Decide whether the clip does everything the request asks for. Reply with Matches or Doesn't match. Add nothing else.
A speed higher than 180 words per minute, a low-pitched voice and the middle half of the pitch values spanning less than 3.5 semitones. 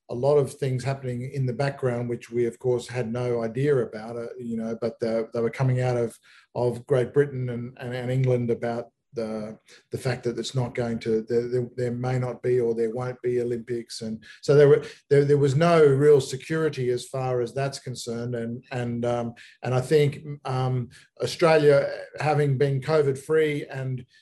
Matches